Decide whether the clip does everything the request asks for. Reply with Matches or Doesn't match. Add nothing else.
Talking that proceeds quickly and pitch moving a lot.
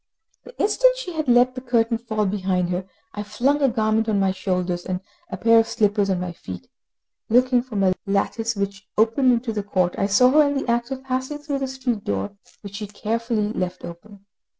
Doesn't match